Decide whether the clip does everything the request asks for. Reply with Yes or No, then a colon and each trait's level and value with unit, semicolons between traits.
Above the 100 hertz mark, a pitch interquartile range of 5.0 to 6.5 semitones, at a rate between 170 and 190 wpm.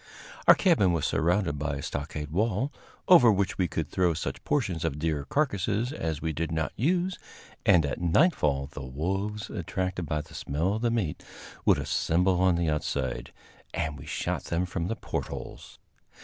No: very low, 85 Hz; average, 5.3 semitones; average, 175 wpm